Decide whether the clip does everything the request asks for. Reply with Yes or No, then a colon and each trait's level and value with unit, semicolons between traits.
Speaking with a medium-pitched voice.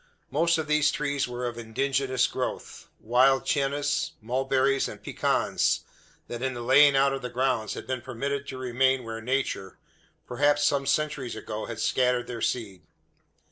No: low, 130 Hz